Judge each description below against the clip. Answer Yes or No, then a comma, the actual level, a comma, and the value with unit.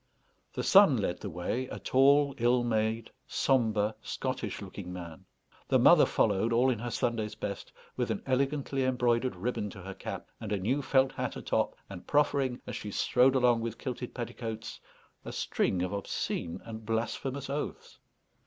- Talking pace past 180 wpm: No, average, 165 wpm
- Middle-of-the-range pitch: No, low, 120 Hz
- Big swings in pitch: No, average, 3.8 semitones